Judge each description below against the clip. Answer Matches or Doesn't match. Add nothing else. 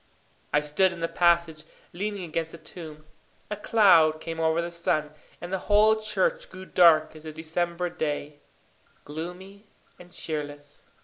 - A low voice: Doesn't match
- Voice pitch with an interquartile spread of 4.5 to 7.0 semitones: Doesn't match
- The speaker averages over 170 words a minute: Doesn't match